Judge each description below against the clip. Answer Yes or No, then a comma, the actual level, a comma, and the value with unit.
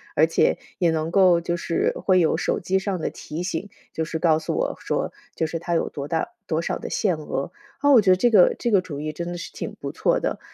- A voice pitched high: No, medium, 170 Hz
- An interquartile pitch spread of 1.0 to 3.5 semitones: Yes, average, 2.7 semitones